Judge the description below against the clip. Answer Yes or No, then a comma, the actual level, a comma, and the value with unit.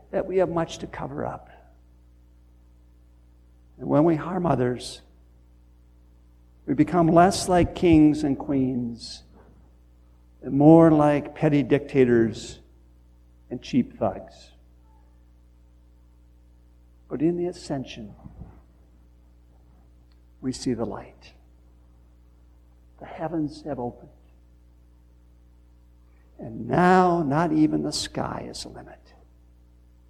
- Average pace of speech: No, slow, 95 wpm